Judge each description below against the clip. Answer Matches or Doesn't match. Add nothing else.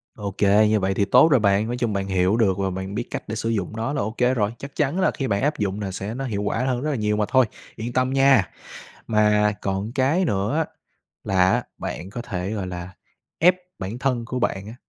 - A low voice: Matches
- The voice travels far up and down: Doesn't match